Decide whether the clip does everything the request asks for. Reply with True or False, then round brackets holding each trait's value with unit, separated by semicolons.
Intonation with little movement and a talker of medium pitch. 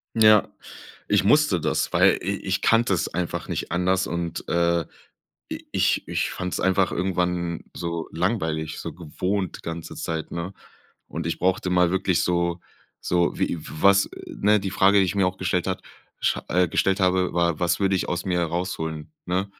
False (2.0 semitones; 90 Hz)